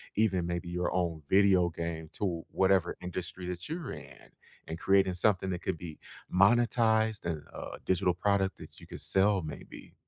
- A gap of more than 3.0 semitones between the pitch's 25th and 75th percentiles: No, narrow, 2.5 semitones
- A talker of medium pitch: No, very low, 90 Hz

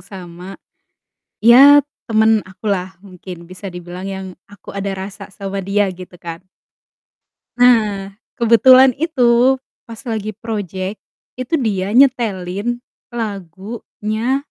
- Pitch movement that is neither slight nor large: Yes, average, 3.7 semitones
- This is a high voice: Yes, high, 200 Hz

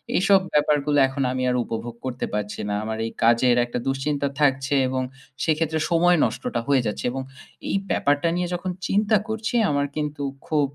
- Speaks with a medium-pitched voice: Yes, medium, 145 Hz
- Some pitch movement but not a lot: Yes, average, 4.1 semitones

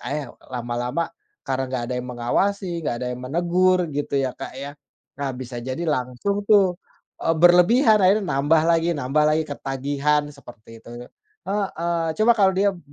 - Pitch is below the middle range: No, medium, 150 Hz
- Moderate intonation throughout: No, wide, 5.8 semitones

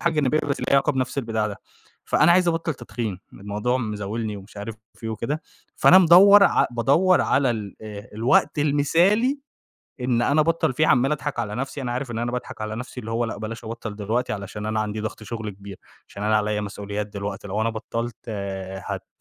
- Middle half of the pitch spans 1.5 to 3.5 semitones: No, average, 5.0 semitones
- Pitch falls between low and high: No, low, 115 Hz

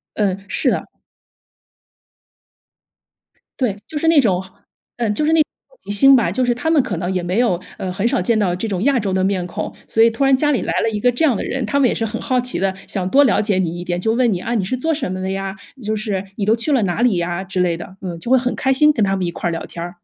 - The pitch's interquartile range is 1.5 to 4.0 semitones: No, average, 5.1 semitones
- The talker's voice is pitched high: Yes, high, 210 Hz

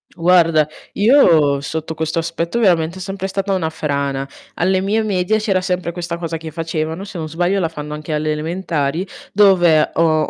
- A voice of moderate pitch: Yes, medium, 165 Hz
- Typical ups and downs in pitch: Yes, average, 3.2 semitones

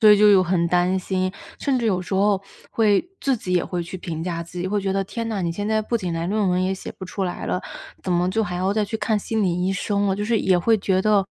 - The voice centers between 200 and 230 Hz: No, high, 190 Hz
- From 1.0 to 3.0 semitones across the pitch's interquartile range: Yes, average, 2.7 semitones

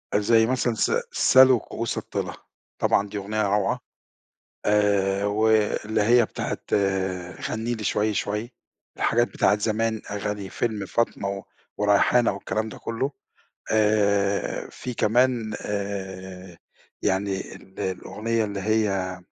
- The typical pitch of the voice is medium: No, low, 105 Hz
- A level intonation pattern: Yes, narrow, 2.0 semitones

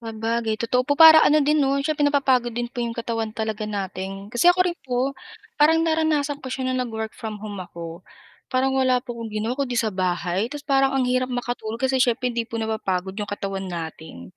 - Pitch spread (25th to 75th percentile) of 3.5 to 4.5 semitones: Yes, average, 4.0 semitones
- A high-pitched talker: Yes, high, 235 Hz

